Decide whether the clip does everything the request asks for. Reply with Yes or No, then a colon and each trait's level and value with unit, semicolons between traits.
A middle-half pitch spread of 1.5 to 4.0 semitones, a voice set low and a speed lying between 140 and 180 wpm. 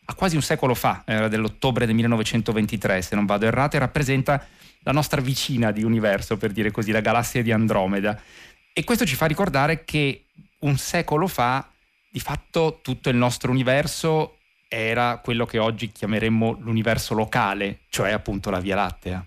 No: average, 4.5 semitones; low, 120 Hz; average, 165 wpm